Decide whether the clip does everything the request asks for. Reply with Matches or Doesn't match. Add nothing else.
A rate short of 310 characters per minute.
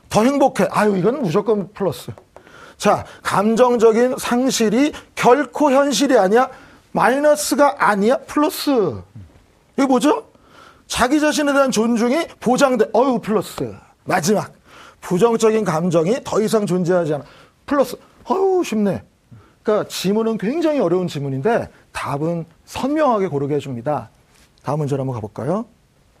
Matches